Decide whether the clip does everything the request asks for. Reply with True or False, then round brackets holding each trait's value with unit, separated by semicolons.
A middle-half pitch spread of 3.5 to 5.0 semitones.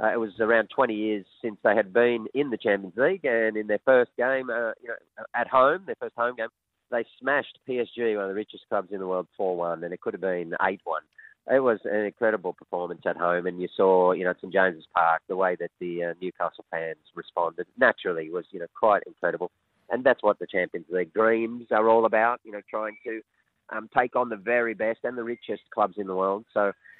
True (4.0 semitones)